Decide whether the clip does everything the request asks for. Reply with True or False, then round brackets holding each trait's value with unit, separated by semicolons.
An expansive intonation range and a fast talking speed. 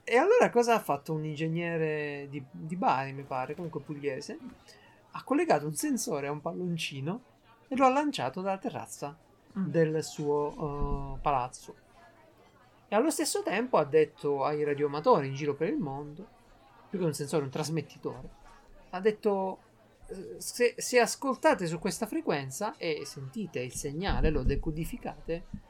False (6.0 semitones; 150 wpm)